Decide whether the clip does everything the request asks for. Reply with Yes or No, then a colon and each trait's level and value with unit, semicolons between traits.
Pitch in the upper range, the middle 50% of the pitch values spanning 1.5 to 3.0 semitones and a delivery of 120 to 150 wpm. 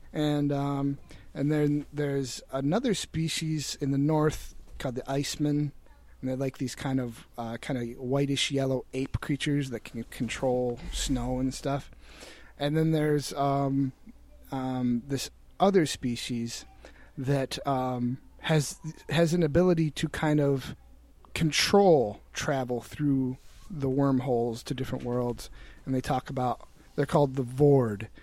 No: medium, 140 Hz; narrow, 2.5 semitones; average, 140 wpm